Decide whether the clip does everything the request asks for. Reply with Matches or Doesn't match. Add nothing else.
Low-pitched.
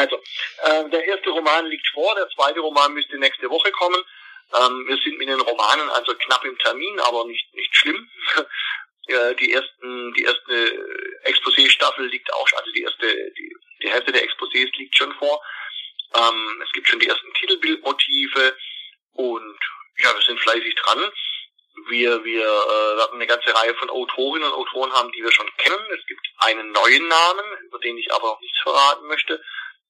Doesn't match